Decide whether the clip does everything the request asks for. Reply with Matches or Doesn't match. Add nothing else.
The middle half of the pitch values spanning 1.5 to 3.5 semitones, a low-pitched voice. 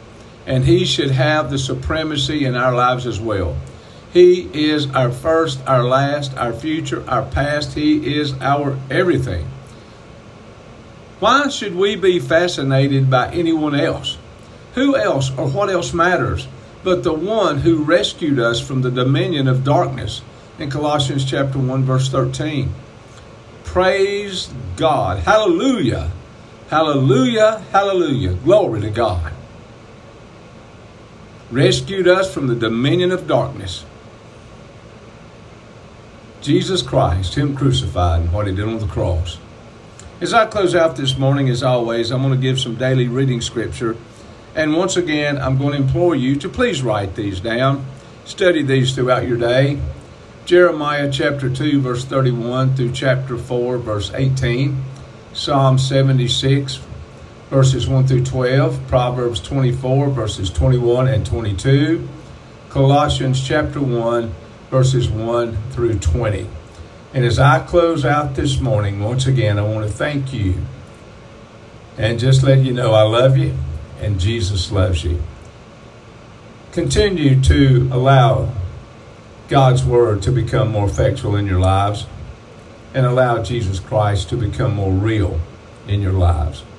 Doesn't match